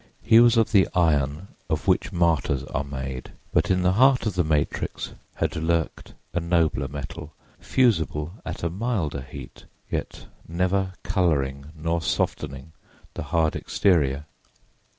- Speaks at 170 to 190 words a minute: No, average, 140 wpm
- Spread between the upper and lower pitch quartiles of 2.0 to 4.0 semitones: No, average, 4.4 semitones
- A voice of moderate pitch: No, very low, 85 Hz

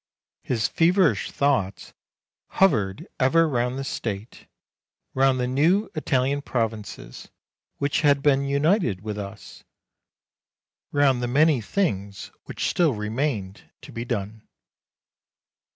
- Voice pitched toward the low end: Yes, low, 130 Hz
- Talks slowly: Yes, slow, 110 wpm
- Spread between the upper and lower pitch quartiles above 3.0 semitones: Yes, average, 5.2 semitones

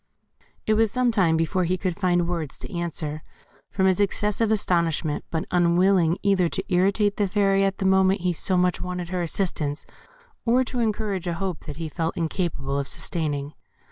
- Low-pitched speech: No, medium, 180 Hz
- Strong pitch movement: No, average, 2.9 semitones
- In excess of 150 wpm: Yes, average, 180 wpm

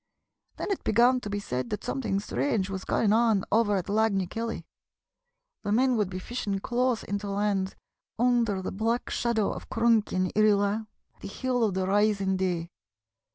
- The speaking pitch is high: Yes, high, 210 Hz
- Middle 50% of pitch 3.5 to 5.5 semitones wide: No, average, 3.0 semitones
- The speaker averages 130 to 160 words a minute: No, average, 185 wpm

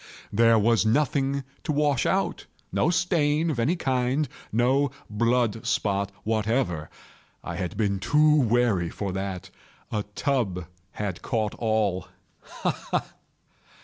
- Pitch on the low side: Yes, low, 115 Hz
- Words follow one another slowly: Yes, slow, 115 wpm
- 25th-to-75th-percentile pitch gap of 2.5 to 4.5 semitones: No, wide, 5.6 semitones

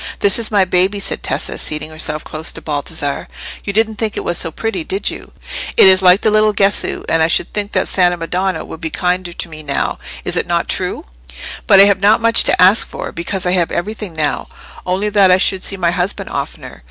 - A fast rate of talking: Yes, fast, 225 wpm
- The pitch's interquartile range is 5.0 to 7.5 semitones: No, average, 3.5 semitones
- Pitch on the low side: No, medium, 185 Hz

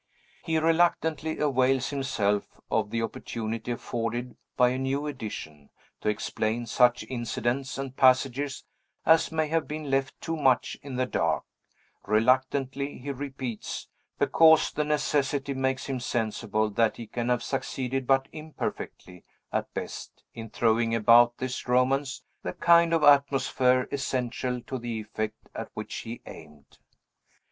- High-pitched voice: No, low, 130 Hz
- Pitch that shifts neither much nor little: Yes, average, 3.3 semitones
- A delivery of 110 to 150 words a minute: Yes, slow, 135 wpm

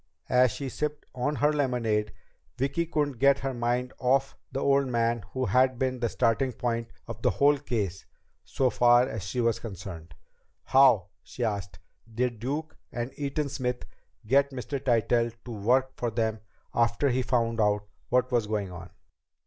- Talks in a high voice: No, low, 125 Hz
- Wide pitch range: No, average, 2.9 semitones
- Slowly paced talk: No, average, 165 wpm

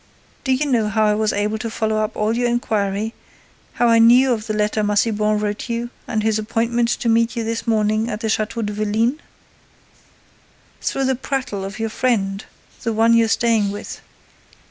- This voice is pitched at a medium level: No, high, 220 Hz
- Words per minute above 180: Yes, average, 190 wpm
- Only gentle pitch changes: Yes, narrow, 1.8 semitones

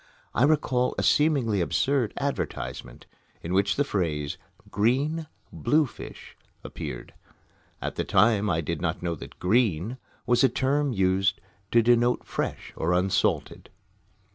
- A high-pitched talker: No, low, 115 Hz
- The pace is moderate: No, slow, 130 wpm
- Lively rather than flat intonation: Yes, wide, 6.5 semitones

